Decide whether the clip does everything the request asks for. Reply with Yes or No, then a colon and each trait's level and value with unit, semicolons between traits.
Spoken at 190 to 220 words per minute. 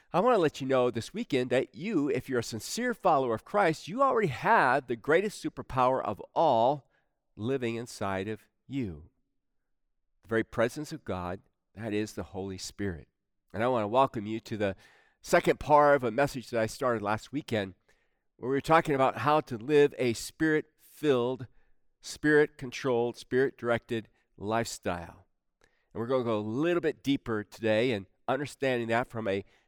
No: average, 170 wpm